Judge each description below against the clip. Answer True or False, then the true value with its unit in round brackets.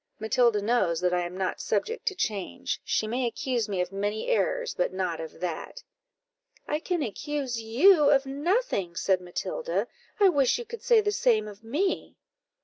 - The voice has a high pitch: True (240 Hz)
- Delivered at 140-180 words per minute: True (175 wpm)